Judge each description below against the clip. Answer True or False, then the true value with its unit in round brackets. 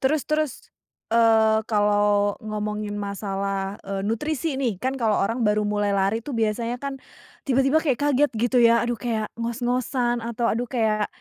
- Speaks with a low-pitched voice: False (230 Hz)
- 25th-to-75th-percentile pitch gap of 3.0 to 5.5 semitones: True (3.3 semitones)